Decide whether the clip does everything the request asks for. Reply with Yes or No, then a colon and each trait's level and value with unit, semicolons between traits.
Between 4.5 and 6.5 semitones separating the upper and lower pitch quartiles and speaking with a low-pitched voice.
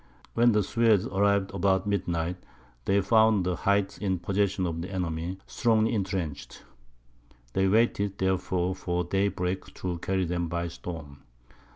No: narrow, 2.4 semitones; very low, 95 Hz